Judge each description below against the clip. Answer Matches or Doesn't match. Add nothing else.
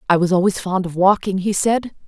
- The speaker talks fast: Matches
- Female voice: Matches